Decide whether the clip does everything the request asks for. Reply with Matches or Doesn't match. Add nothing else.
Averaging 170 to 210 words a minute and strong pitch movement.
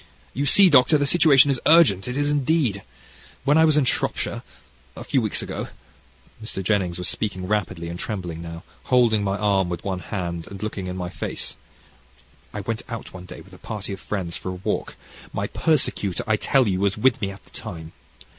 Matches